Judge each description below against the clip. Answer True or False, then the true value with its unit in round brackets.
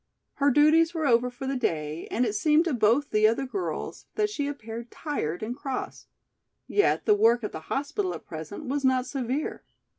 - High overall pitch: True (260 Hz)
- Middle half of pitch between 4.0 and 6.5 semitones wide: True (4.7 semitones)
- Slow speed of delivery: False (190 wpm)